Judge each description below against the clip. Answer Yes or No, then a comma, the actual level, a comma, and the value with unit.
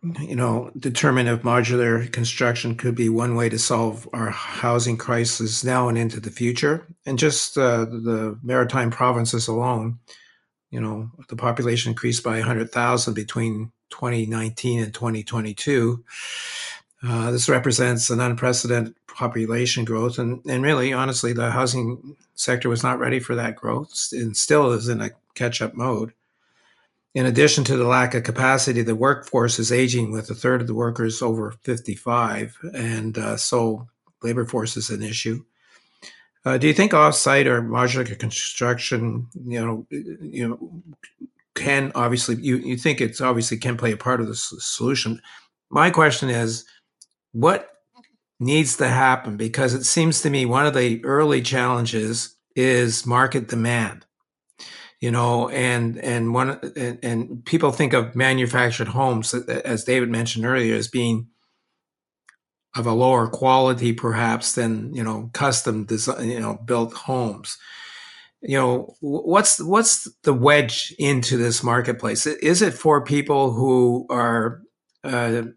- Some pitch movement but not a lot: No, narrow, 2.2 semitones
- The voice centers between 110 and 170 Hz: Yes, low, 120 Hz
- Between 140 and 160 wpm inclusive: Yes, average, 150 wpm